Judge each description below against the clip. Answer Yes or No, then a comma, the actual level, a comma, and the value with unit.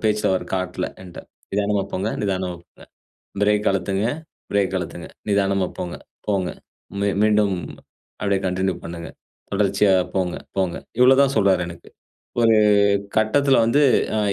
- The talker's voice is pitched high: No, low, 100 Hz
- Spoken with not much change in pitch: Yes, narrow, 2.2 semitones